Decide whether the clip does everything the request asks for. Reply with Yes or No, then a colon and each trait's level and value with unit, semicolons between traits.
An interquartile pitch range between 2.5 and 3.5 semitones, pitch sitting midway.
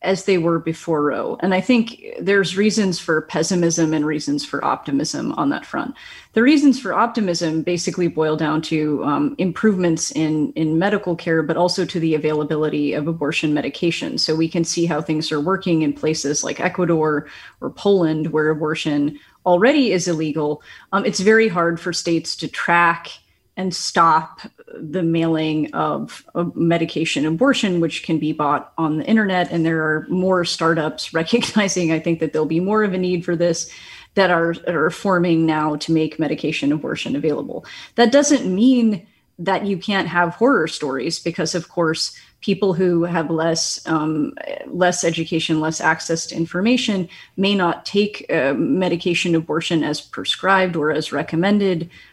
Yes: average, 3.0 semitones; medium, 170 Hz